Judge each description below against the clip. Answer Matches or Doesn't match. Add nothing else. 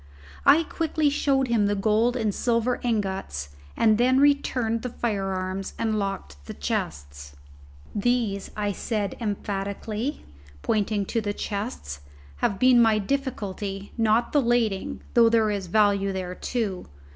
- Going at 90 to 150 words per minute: Matches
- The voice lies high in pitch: Matches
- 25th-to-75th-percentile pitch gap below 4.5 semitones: Matches